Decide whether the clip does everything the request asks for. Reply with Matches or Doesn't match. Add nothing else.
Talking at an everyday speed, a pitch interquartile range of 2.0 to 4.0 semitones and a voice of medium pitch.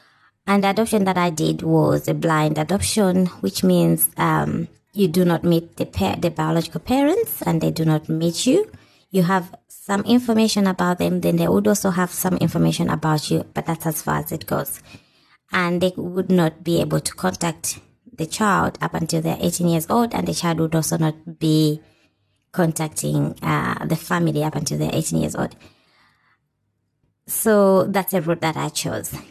Matches